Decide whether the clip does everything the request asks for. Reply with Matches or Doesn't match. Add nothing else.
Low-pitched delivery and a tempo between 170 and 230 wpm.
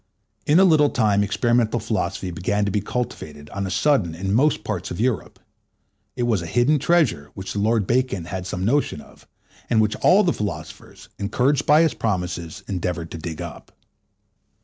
Matches